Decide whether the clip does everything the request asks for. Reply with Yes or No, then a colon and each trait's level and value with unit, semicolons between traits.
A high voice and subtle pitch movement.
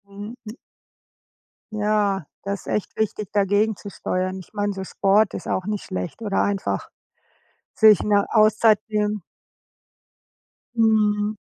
Yes: high, 210 Hz; narrow, 1.4 semitones